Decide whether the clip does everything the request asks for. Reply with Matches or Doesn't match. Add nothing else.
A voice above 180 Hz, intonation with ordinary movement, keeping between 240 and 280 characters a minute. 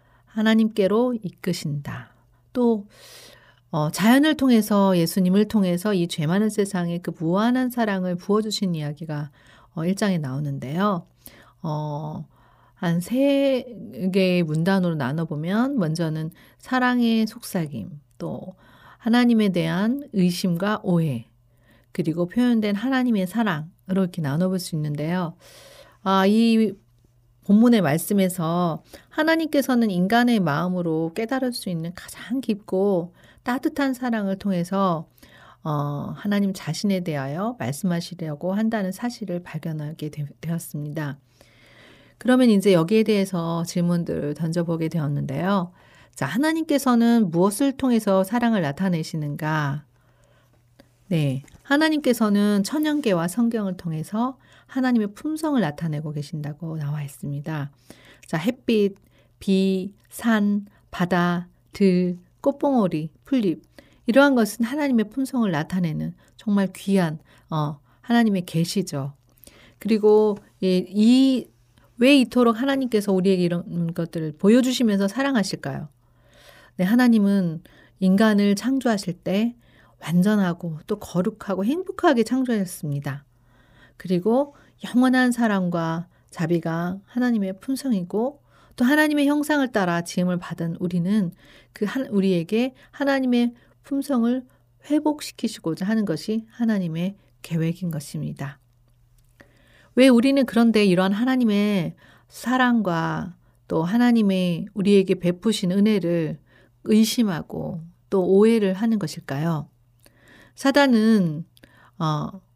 Doesn't match